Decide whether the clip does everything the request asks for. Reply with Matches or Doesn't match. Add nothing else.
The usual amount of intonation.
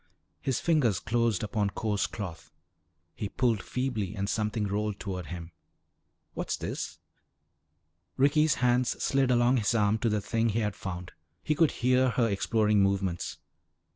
Matches